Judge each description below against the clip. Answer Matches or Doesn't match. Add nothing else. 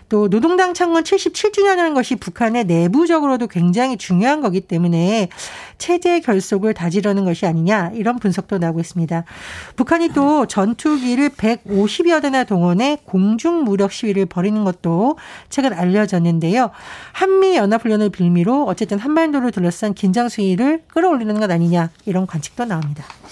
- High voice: Matches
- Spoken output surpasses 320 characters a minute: Matches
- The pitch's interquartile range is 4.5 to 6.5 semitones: Doesn't match